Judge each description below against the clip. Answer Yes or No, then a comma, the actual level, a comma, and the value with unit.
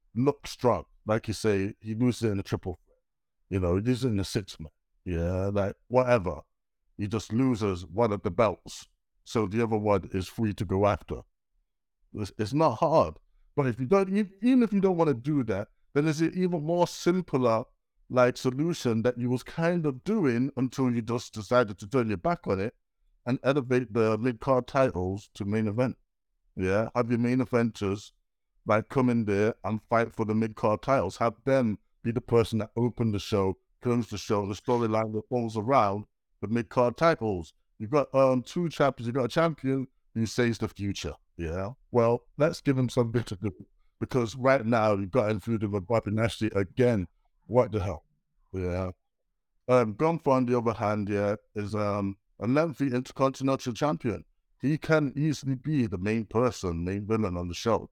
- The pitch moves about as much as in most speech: Yes, average, 4.1 semitones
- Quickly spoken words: No, average, 185 wpm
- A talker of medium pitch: No, low, 115 Hz